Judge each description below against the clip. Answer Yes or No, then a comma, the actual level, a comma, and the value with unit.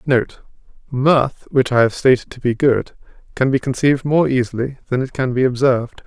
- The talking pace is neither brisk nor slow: Yes, average, 180 wpm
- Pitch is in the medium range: No, low, 130 Hz